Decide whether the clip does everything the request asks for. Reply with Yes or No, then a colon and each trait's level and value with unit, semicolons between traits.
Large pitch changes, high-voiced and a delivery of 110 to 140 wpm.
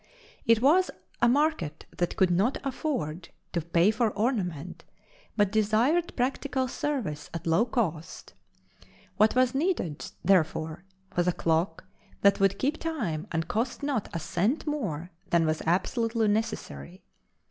Yes: wide, 7.1 semitones; high, 210 Hz; slow, 135 wpm